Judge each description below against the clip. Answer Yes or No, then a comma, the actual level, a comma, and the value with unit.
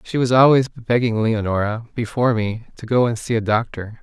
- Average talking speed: Yes, average, 195 wpm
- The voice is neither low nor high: No, low, 115 Hz